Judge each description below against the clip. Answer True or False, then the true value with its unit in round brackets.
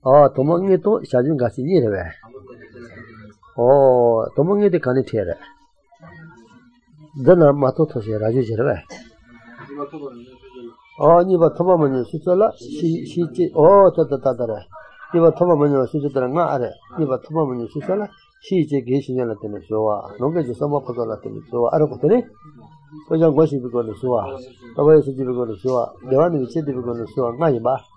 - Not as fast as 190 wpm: False (195 wpm)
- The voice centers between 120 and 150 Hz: True (140 Hz)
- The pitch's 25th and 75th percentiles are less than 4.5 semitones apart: False (5.1 semitones)